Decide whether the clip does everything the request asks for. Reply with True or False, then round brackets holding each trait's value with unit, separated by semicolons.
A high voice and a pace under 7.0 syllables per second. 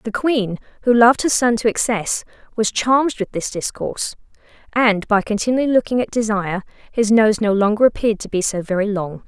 True (220 Hz; 5.8 syllables/s)